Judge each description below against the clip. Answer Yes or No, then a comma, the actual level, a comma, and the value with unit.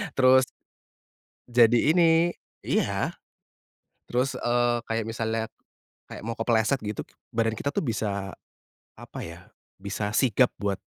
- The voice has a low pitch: Yes, low, 115 Hz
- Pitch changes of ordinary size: Yes, average, 3.0 semitones